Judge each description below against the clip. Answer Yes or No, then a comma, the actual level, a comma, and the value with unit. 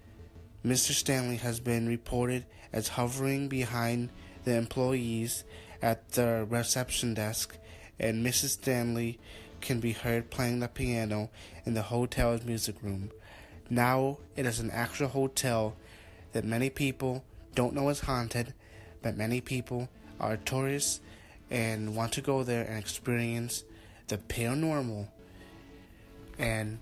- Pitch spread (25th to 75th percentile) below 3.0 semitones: Yes, narrow, 2.5 semitones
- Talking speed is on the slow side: Yes, slow, 125 wpm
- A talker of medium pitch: No, low, 115 Hz